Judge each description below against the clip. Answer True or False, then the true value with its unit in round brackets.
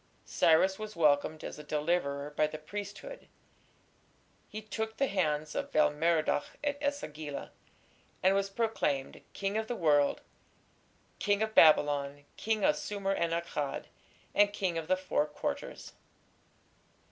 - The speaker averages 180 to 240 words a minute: False (140 wpm)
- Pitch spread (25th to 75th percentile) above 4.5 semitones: True (5.4 semitones)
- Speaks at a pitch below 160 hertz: False (170 Hz)